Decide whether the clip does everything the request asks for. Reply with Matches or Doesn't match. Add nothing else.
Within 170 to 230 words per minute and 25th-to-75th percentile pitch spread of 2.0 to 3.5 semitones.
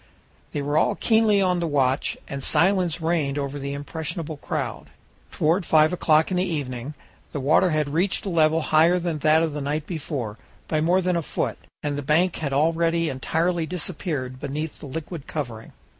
Matches